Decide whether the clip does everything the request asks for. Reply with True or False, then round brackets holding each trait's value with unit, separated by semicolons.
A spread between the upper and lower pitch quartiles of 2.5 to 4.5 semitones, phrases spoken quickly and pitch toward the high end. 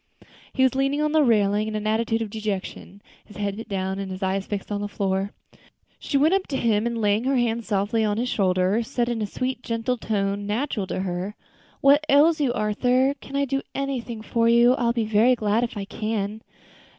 True (3.5 semitones; 220 wpm; 225 Hz)